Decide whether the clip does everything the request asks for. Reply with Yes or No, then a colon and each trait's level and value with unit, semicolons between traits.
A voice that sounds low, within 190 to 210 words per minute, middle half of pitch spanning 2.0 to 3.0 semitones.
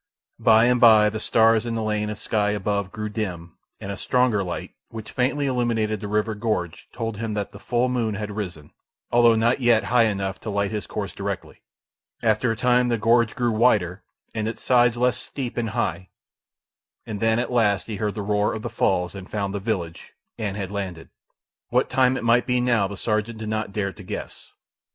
Yes: low, 110 Hz; fast, 205 wpm; narrow, 2.6 semitones